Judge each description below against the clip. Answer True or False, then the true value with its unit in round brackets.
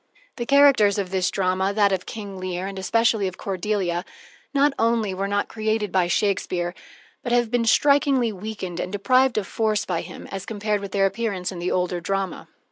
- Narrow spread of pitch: False (3.3 semitones)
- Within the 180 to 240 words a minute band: True (190 wpm)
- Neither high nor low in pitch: False (200 Hz)